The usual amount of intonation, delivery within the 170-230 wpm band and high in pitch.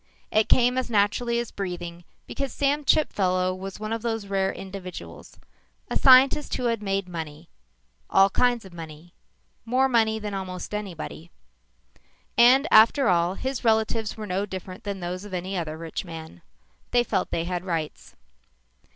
No: average, 4.6 semitones; average, 160 wpm; high, 195 Hz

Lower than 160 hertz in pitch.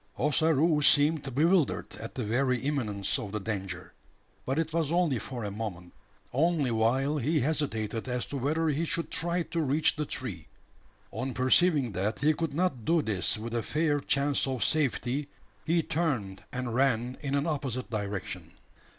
Yes: low, 135 Hz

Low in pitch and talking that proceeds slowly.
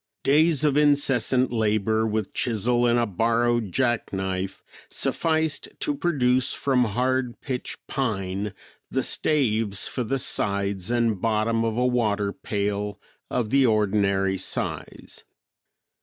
Yes: low, 115 Hz; slow, 120 wpm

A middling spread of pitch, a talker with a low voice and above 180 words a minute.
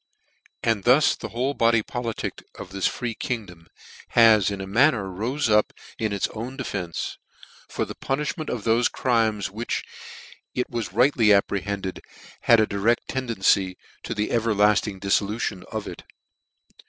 No: average, 3.3 semitones; low, 110 Hz; average, 155 wpm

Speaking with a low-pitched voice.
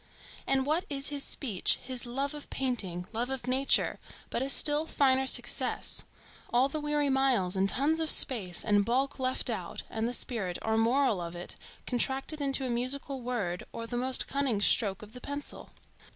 No: very high, 255 Hz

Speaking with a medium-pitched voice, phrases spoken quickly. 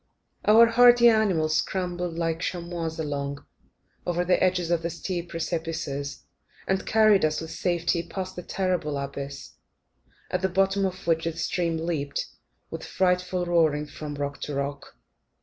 No: medium, 170 Hz; average, 150 wpm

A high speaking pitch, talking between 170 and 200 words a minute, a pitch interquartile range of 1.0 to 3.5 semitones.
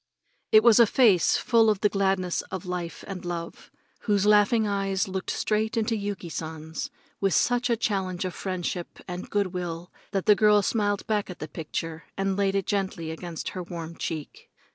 Yes: high, 195 Hz; average, 185 wpm; average, 3.0 semitones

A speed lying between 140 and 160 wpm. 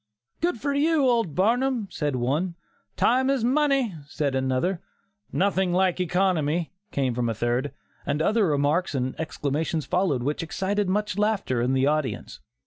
Yes: average, 150 wpm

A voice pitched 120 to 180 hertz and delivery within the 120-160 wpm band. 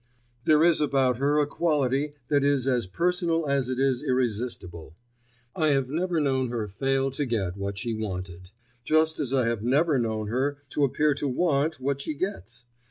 No: low, 135 Hz; average, 180 wpm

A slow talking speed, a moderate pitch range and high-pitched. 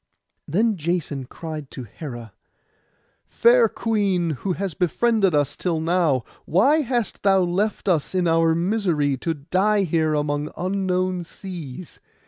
No: slow, 130 wpm; average, 4.5 semitones; medium, 175 Hz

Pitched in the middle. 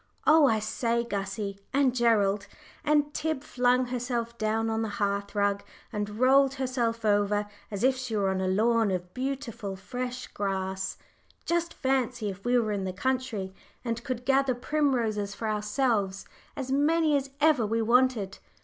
No: high, 230 Hz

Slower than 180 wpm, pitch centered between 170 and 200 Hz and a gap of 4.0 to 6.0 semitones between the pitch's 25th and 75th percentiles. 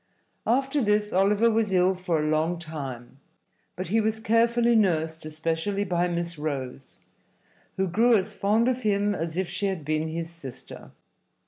Yes: average, 160 wpm; medium, 185 Hz; average, 4.9 semitones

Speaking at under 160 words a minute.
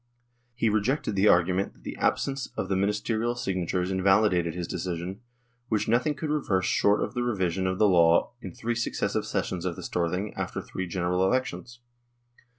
No: average, 180 wpm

